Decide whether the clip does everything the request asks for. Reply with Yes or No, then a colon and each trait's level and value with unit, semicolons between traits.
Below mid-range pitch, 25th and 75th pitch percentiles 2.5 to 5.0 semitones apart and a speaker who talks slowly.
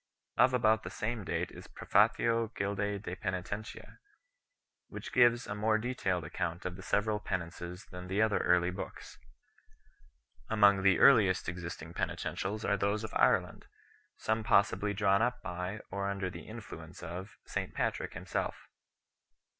No: low, 100 Hz; average, 3.1 semitones; average, 160 wpm